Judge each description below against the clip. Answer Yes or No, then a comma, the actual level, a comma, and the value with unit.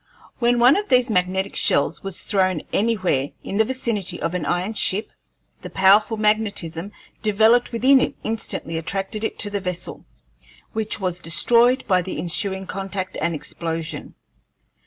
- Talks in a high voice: Yes, high, 195 Hz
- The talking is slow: No, average, 150 wpm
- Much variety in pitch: No, average, 3.7 semitones